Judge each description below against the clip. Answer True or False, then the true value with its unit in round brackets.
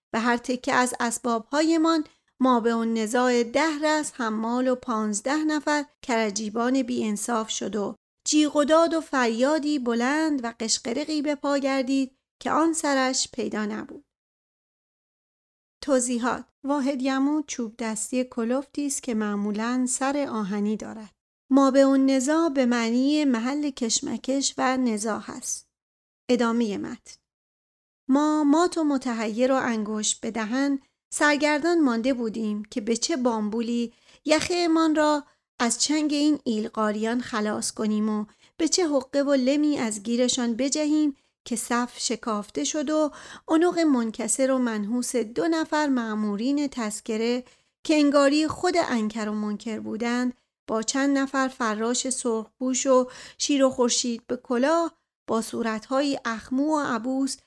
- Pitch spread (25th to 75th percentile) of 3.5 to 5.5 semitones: True (4.0 semitones)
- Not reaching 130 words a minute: False (135 wpm)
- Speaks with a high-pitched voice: True (255 Hz)